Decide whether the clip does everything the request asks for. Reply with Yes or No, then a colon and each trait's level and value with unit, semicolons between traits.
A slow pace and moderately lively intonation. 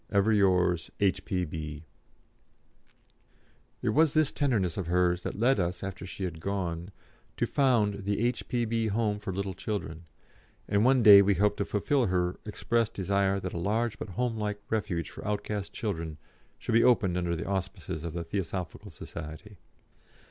No: average, 155 wpm; average, 3.4 semitones